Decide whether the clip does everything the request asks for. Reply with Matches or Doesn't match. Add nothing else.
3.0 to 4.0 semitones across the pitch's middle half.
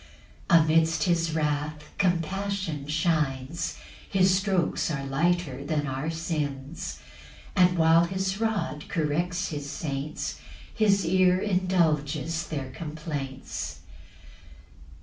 Matches